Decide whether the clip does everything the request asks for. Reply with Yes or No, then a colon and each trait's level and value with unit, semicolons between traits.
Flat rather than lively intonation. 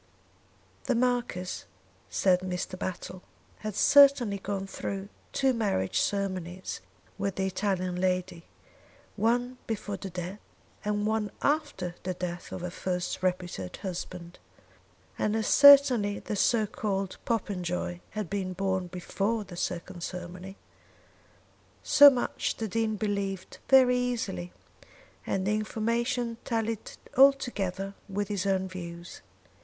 No: average, 3.5 semitones